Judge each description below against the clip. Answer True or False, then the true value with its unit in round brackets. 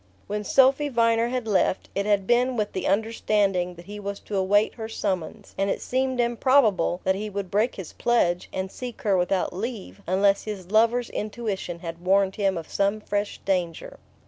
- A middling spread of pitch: True (3.3 semitones)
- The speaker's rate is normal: True (185 wpm)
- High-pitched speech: True (205 Hz)